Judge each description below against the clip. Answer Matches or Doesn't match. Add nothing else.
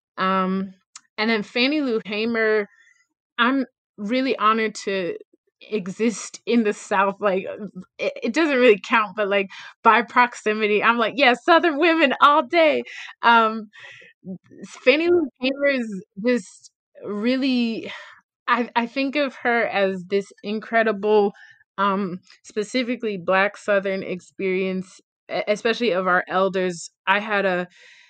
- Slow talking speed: Matches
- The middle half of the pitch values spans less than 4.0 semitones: Doesn't match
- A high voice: Matches